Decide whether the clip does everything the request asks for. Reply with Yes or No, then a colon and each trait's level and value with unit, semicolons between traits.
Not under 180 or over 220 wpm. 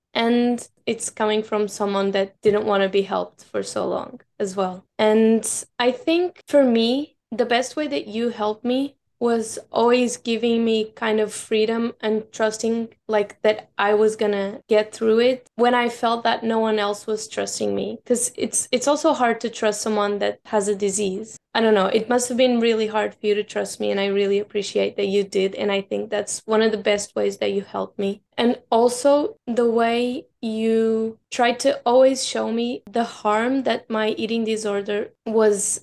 Yes: average, 200 wpm